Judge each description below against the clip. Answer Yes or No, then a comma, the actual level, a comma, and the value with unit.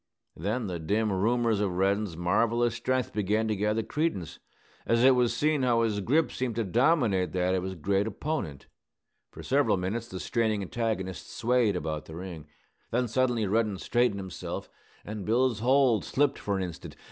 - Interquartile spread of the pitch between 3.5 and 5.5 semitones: Yes, average, 4.3 semitones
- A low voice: Yes, low, 110 Hz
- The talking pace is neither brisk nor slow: Yes, average, 170 wpm